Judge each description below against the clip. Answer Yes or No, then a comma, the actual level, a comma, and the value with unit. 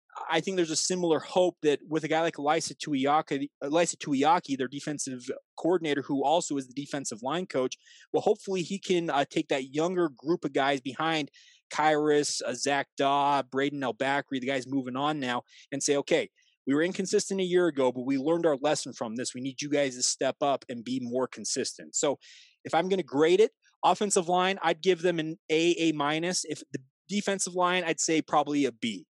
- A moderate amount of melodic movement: Yes, average, 4.2 semitones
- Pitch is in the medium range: Yes, medium, 155 Hz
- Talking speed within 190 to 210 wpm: Yes, fast, 205 wpm